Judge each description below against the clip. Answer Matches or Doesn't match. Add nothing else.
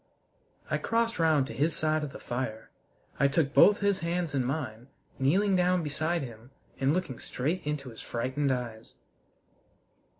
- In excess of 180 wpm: Doesn't match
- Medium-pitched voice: Matches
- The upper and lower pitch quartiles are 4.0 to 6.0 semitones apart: Matches